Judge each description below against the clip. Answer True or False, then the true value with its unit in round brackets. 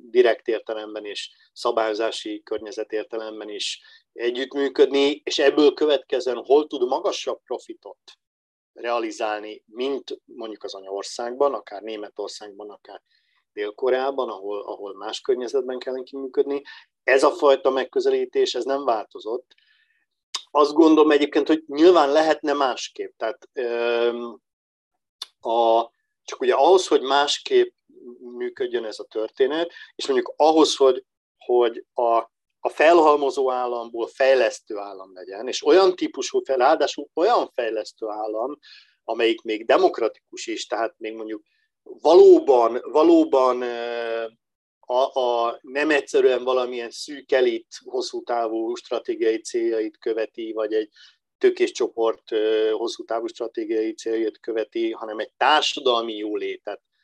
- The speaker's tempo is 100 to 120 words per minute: True (115 wpm)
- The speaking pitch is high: True (355 Hz)